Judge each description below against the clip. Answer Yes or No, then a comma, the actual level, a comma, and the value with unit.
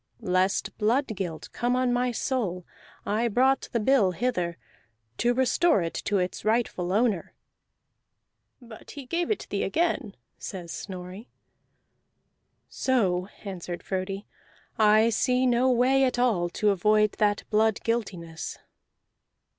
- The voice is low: No, high, 215 Hz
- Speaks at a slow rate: Yes, slow, 125 wpm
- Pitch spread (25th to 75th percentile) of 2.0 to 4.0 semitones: No, average, 4.9 semitones